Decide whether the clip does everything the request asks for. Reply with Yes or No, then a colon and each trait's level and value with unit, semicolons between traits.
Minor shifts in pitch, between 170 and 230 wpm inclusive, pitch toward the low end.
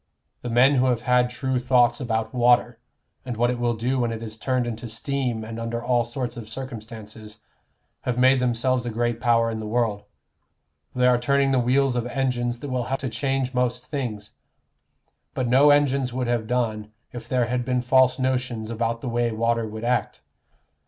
Yes: narrow, 1.8 semitones; average, 195 wpm; low, 120 Hz